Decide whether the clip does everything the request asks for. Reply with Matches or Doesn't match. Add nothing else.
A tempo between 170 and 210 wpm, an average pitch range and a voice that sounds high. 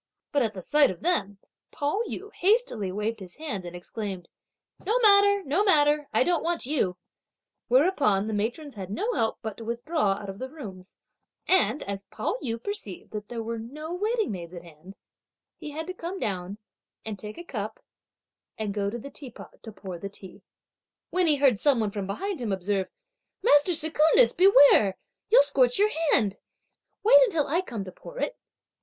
Doesn't match